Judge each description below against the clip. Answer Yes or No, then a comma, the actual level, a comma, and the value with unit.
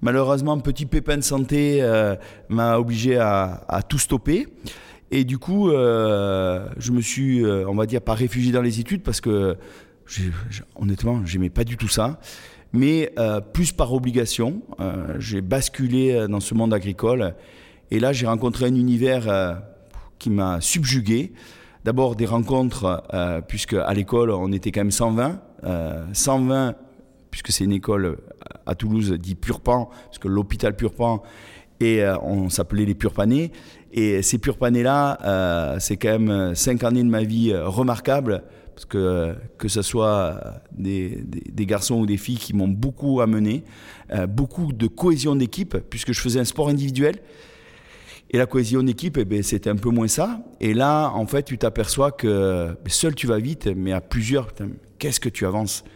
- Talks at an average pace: Yes, average, 170 wpm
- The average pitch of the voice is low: Yes, low, 115 Hz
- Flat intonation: No, average, 4.3 semitones